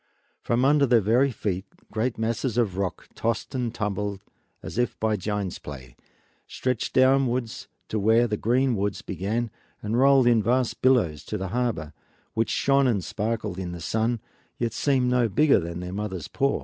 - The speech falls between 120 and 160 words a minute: No, average, 175 wpm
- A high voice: No, low, 115 Hz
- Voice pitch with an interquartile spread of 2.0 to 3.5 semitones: No, average, 4.0 semitones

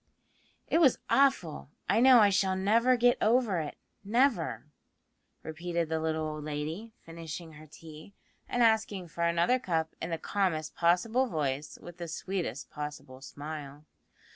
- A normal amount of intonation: No, wide, 5.8 semitones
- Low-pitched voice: No, medium, 170 Hz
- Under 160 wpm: Yes, average, 145 wpm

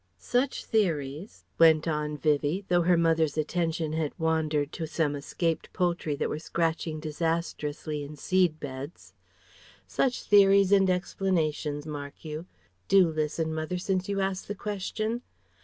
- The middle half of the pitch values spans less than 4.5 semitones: Yes, average, 3.4 semitones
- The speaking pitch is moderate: Yes, medium, 160 Hz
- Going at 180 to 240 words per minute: No, average, 140 wpm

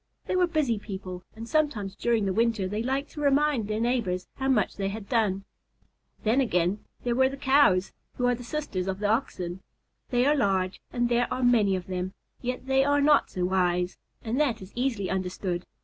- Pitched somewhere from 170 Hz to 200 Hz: No, high, 225 Hz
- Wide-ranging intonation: Yes, wide, 5.7 semitones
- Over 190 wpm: Yes, average, 200 wpm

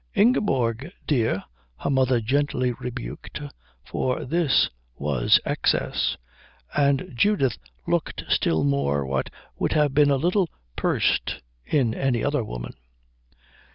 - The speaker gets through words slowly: Yes, slow, 115 wpm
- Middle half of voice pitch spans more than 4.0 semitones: Yes, average, 5.0 semitones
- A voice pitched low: Yes, low, 130 Hz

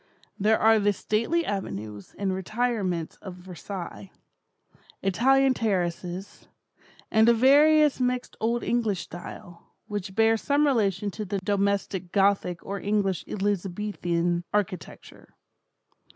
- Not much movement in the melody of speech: No, average, 3.7 semitones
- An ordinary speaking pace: No, slow, 110 wpm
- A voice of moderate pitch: No, high, 200 Hz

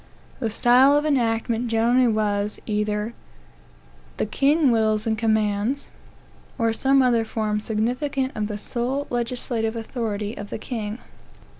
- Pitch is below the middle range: No, high, 225 Hz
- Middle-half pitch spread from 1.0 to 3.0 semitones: Yes, average, 2.7 semitones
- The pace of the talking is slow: Yes, slow, 130 wpm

